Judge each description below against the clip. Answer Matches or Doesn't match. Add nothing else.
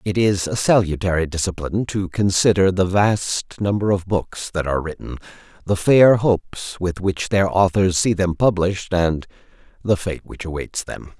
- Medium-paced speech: Matches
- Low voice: Matches